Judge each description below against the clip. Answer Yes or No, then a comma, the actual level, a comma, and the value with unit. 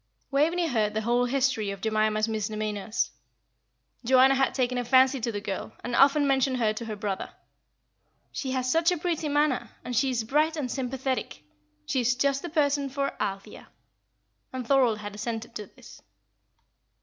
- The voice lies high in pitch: Yes, very high, 250 Hz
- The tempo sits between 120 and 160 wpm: No, average, 170 wpm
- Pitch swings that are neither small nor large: Yes, average, 4.1 semitones